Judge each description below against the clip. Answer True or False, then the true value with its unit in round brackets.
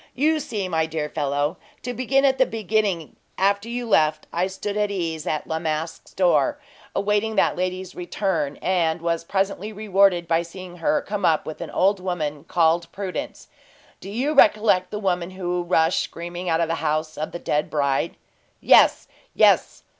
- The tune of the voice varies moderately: True (3.9 semitones)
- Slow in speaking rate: False (175 wpm)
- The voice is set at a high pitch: False (180 Hz)